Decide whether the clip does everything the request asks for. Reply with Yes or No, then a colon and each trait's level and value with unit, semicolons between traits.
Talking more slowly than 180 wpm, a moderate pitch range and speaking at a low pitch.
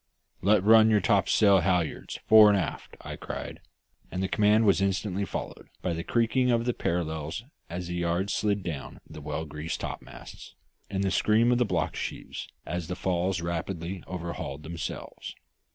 Yes: average, 170 wpm; average, 3.6 semitones; very low, 95 Hz